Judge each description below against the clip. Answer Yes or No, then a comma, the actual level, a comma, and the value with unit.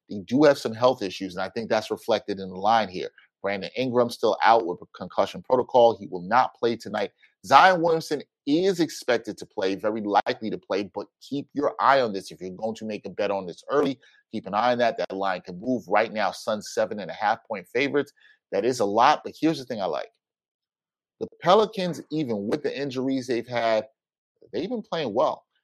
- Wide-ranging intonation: Yes, wide, 7.7 semitones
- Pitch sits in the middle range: No, low, 125 Hz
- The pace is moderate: No, fast, 220 wpm